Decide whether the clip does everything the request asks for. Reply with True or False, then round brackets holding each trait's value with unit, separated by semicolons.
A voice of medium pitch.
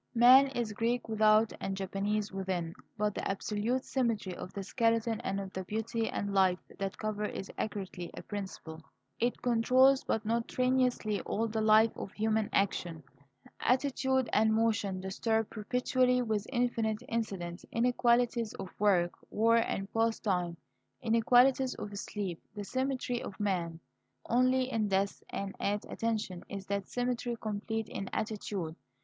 False (215 Hz)